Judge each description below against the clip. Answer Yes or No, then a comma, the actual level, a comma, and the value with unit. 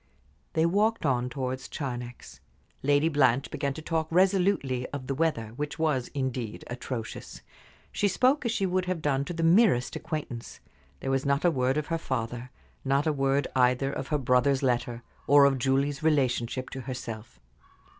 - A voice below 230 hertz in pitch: Yes, medium, 140 Hz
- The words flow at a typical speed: Yes, average, 170 wpm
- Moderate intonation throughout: Yes, average, 4.0 semitones